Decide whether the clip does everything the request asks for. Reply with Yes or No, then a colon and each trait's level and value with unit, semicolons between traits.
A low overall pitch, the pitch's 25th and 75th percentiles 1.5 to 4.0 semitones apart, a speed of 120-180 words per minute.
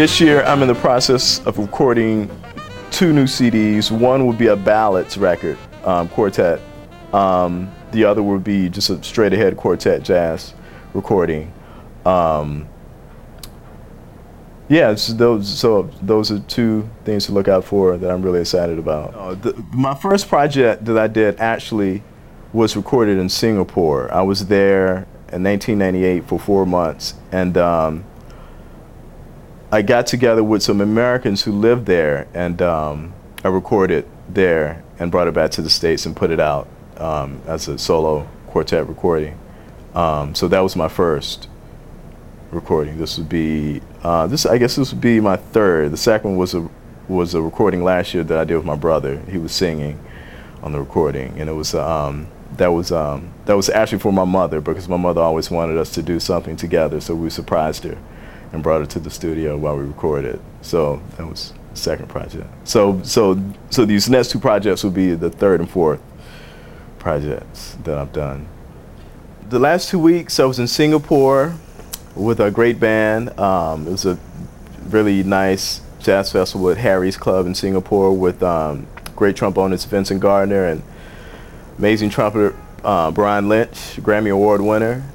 No: very low, 95 Hz; average, 4.5 semitones; average, 170 wpm